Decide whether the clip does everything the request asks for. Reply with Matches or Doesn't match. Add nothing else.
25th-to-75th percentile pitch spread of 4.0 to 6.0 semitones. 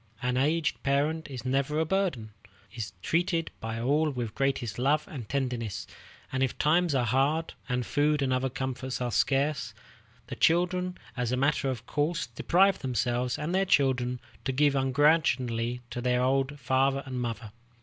Doesn't match